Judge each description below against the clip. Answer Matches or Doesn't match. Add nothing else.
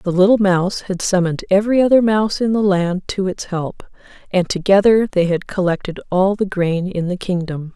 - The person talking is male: Doesn't match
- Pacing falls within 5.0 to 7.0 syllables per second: Matches